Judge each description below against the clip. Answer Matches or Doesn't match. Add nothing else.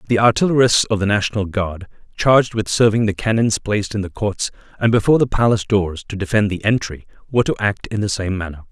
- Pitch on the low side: Matches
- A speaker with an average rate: Doesn't match